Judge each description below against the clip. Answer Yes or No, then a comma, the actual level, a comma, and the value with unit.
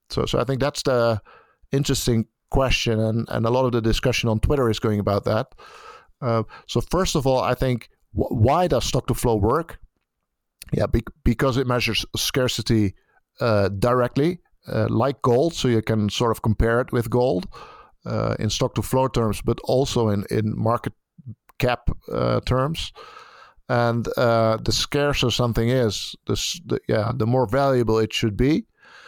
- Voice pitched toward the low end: Yes, low, 120 Hz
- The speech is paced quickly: No, average, 175 wpm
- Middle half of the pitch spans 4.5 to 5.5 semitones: No, average, 2.7 semitones